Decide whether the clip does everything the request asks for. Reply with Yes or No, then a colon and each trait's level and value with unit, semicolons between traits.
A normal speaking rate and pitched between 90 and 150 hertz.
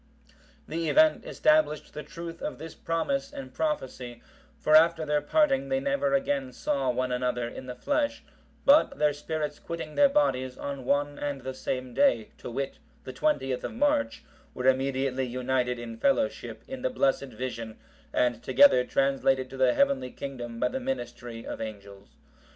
Yes: average, 165 wpm; medium, 140 Hz